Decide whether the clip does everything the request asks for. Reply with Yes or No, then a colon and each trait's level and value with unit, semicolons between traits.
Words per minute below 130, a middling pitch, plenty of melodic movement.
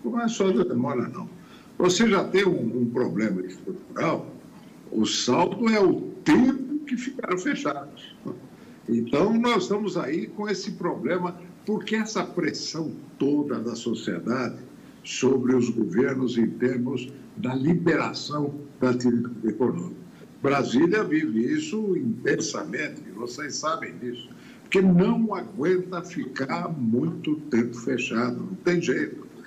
Yes: slow, 120 wpm; medium, 170 Hz; wide, 8.5 semitones